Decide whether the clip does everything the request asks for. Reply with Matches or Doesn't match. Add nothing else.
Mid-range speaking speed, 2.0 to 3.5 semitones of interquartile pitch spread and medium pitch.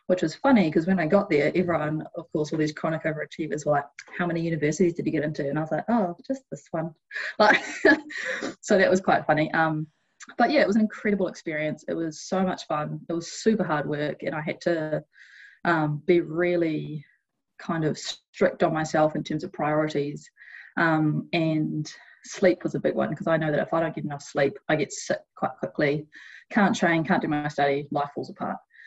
Doesn't match